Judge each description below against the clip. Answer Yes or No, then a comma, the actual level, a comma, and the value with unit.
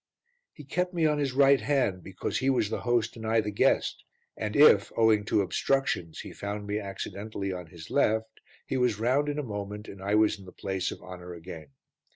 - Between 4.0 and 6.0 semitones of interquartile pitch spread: Yes, average, 4.8 semitones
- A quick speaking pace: Yes, fast, 210 wpm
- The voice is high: No, low, 105 Hz